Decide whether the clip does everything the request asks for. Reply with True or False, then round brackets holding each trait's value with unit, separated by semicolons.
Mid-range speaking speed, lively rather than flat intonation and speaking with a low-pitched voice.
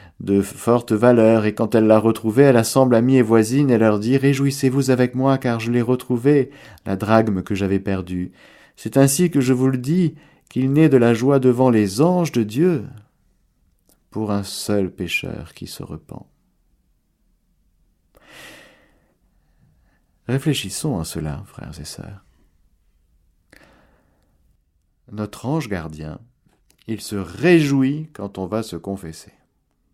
False (140 wpm; 6.0 semitones; 110 Hz)